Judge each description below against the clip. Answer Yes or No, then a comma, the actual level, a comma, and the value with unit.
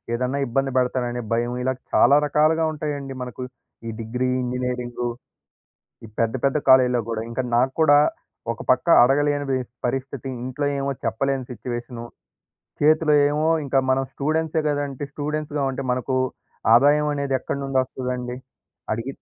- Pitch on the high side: No, low, 135 Hz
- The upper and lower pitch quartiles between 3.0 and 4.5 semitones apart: No, narrow, 2.6 semitones